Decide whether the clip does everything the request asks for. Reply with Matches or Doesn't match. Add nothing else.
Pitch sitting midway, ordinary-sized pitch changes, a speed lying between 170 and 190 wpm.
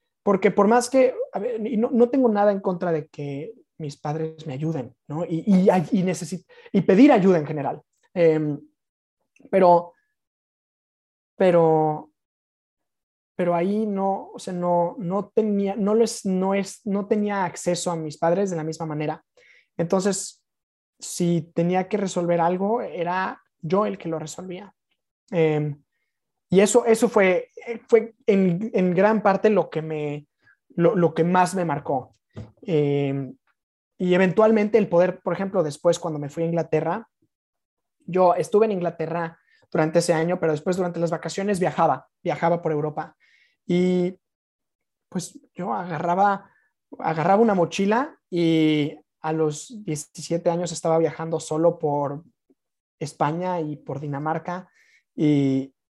Doesn't match